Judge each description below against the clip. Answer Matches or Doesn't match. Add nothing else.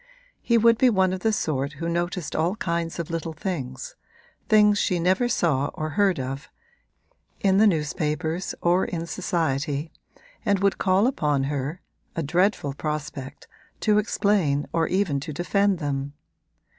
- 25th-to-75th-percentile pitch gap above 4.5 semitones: Matches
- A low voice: Doesn't match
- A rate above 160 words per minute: Doesn't match